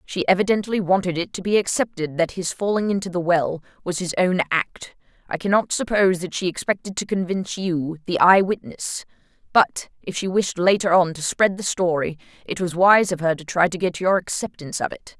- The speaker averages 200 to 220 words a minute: Yes, fast, 205 wpm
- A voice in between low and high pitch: Yes, medium, 180 Hz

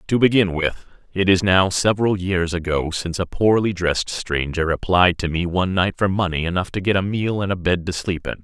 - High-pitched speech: No, very low, 90 Hz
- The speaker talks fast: Yes, fast, 230 wpm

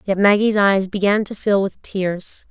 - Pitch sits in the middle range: No, high, 200 Hz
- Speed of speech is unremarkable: Yes, average, 190 wpm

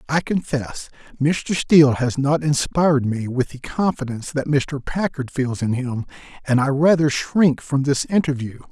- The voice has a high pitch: No, medium, 140 Hz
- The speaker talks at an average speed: Yes, average, 165 wpm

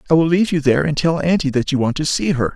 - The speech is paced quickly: Yes, fast, 330 wpm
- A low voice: No, medium, 155 Hz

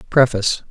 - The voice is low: Yes, low, 120 Hz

